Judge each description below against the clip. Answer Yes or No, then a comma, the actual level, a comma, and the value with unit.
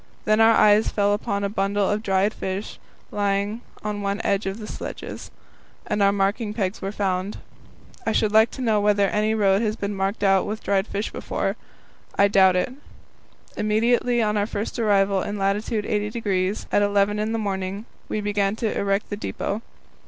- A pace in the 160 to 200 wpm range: Yes, average, 175 wpm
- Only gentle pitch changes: Yes, narrow, 1.4 semitones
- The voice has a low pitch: No, high, 205 Hz